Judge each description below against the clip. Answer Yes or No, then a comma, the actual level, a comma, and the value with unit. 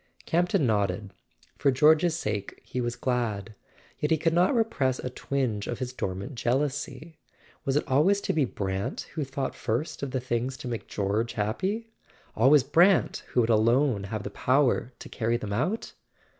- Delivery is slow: No, average, 170 wpm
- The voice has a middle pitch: No, low, 130 Hz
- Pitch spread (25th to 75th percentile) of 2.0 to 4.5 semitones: No, average, 5.3 semitones